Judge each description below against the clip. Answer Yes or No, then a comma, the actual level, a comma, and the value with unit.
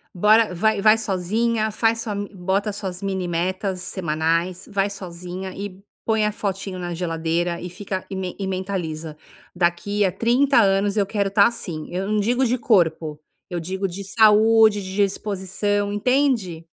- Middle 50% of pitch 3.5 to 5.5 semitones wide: No, average, 2.9 semitones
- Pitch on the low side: No, high, 195 Hz